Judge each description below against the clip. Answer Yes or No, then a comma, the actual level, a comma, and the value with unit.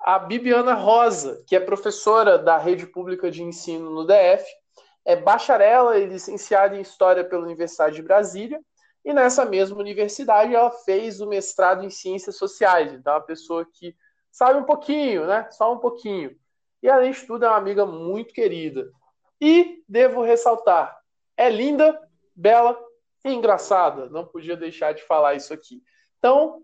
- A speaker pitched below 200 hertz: No, high, 210 Hz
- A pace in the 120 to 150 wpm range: No, average, 160 wpm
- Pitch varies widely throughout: Yes, wide, 5.8 semitones